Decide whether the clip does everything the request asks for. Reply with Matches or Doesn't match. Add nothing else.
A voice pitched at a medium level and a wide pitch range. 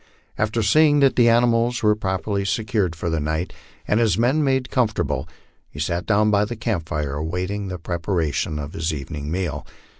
Doesn't match